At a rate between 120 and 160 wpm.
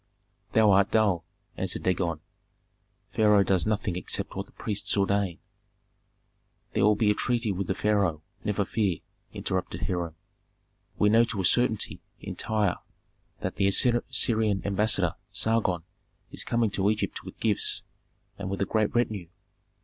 Yes: average, 145 wpm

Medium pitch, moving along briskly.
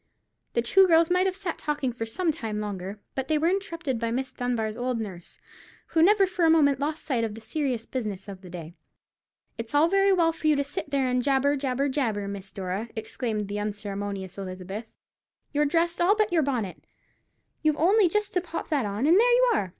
No: very high, 265 Hz; fast, 210 wpm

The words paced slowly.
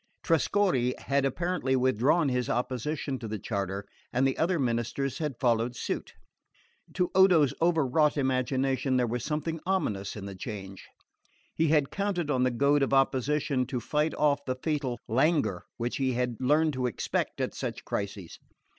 No: average, 160 wpm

